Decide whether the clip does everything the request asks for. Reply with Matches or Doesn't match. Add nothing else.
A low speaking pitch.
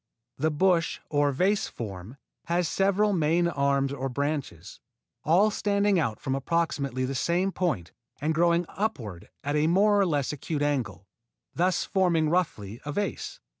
Doesn't match